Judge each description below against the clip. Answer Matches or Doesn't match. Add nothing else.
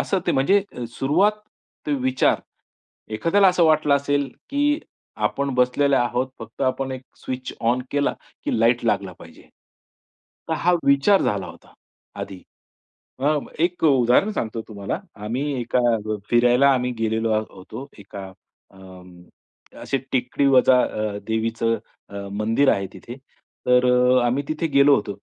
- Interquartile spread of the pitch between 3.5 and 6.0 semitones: Matches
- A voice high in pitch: Doesn't match